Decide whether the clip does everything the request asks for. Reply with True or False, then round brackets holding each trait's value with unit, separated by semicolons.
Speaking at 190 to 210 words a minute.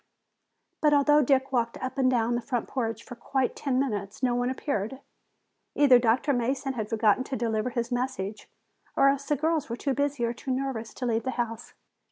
True (200 wpm)